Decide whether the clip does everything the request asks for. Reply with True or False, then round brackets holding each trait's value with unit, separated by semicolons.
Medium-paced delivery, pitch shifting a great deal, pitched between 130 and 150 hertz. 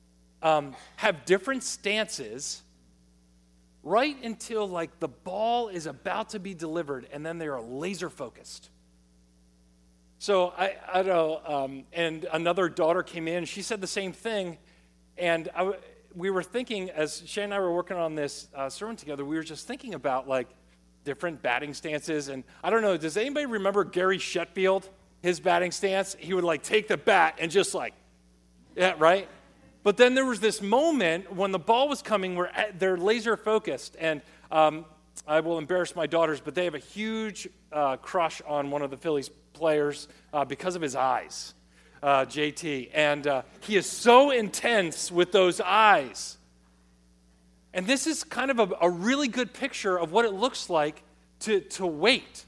False (175 wpm; 5.9 semitones; 170 Hz)